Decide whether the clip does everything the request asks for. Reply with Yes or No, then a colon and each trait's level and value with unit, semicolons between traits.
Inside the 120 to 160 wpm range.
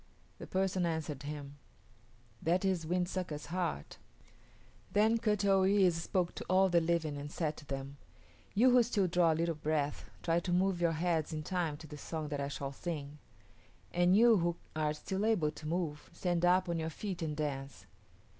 No: average, 190 wpm